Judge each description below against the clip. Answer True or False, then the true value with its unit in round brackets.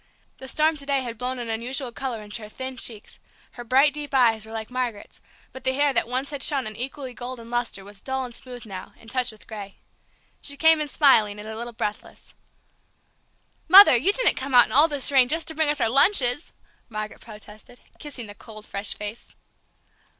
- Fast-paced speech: True (210 wpm)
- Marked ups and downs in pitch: False (3.9 semitones)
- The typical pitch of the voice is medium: False (250 Hz)